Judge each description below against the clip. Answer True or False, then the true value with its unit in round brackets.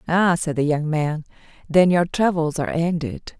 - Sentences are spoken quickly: False (175 wpm)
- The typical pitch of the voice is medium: True (165 Hz)